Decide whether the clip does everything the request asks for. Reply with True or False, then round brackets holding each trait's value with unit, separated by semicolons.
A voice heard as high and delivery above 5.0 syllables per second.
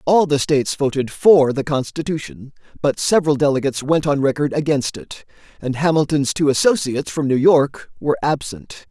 False (145 Hz; 5.4 syllables/s)